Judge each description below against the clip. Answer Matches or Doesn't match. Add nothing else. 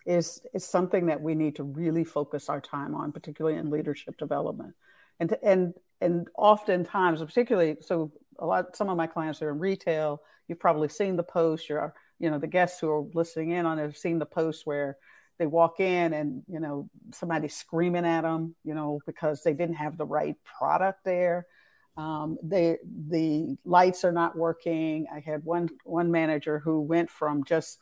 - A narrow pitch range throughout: Matches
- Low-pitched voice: Doesn't match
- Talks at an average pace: Matches